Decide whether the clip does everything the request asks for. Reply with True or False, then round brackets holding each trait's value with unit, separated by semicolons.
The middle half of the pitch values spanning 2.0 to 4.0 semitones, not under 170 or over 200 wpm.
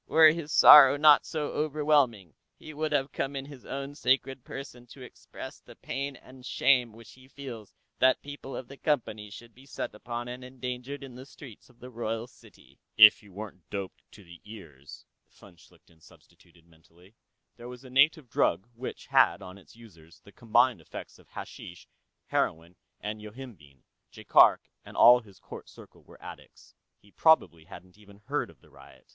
False (5.1 semitones; 180 wpm)